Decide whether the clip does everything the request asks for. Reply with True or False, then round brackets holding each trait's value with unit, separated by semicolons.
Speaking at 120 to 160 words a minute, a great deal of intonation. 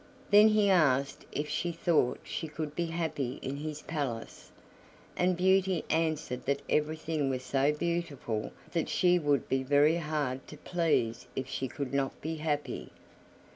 False (155 wpm; 3.6 semitones)